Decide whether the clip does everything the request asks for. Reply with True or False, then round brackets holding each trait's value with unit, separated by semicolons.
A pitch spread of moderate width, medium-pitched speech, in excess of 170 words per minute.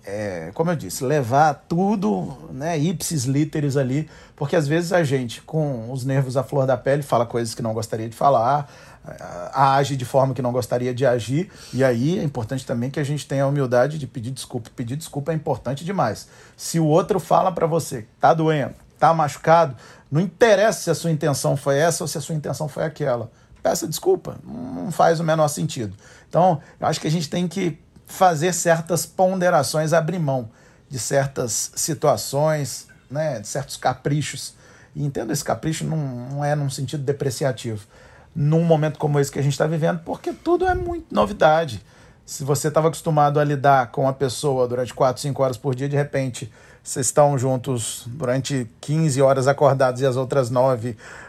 True (3.5 semitones; 145 Hz; 185 wpm)